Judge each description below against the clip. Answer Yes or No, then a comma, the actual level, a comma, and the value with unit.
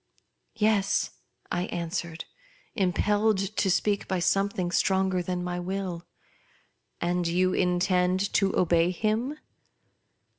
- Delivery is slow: Yes, slow, 115 wpm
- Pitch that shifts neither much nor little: No, narrow, 2.0 semitones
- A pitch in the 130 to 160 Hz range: No, medium, 185 Hz